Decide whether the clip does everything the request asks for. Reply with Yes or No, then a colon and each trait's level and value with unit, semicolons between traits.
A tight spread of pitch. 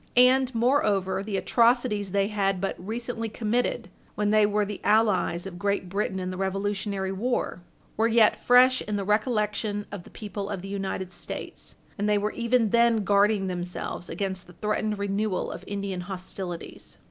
Yes: narrow, 2.3 semitones